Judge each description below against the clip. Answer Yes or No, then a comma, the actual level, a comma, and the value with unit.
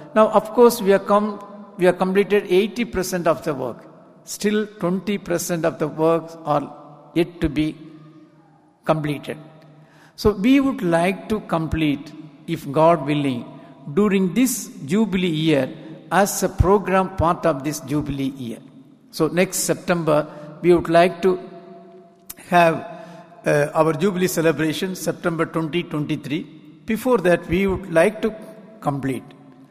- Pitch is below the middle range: No, medium, 170 Hz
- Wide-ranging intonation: No, average, 3.7 semitones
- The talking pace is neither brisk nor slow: No, slow, 130 wpm